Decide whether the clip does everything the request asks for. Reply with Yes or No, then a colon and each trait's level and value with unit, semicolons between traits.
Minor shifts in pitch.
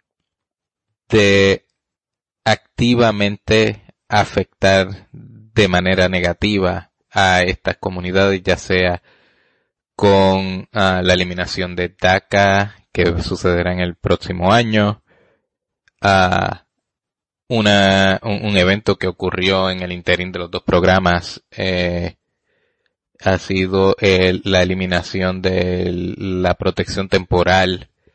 Yes: narrow, 1.6 semitones